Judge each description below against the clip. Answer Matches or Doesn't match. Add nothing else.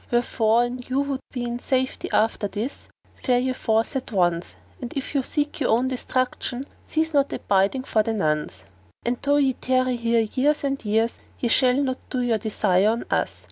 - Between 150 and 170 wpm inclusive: Doesn't match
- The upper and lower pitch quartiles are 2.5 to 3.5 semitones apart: Matches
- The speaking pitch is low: Doesn't match